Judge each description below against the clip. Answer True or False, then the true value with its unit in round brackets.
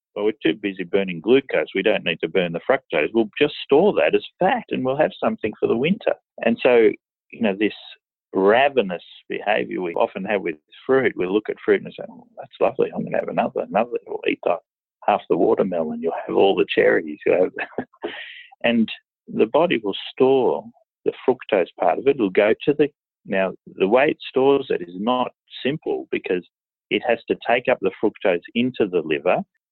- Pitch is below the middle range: False (390 Hz)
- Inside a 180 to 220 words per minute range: True (200 wpm)